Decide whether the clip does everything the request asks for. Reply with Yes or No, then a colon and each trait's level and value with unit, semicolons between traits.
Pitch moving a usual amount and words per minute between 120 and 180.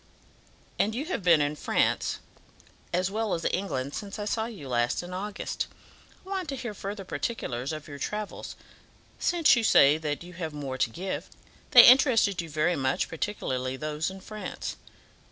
No: wide, 6.3 semitones; average, 170 wpm